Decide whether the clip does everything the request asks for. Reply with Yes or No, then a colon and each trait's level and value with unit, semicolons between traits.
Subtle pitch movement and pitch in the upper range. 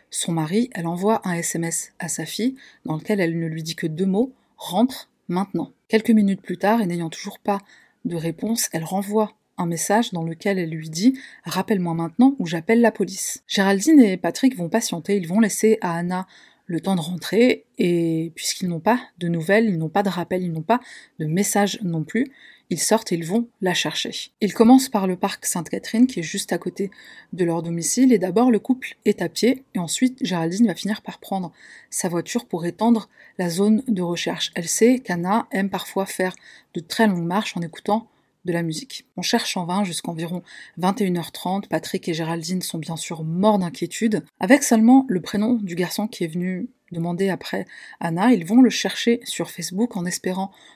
No: average, 4.4 semitones; high, 195 Hz